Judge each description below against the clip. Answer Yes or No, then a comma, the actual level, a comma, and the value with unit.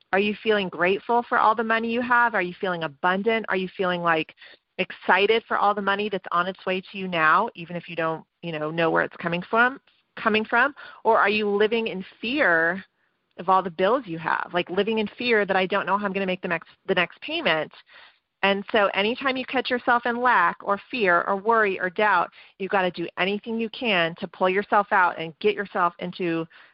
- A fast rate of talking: Yes, fast, 230 wpm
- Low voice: No, high, 195 Hz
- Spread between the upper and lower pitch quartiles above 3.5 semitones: Yes, average, 3.9 semitones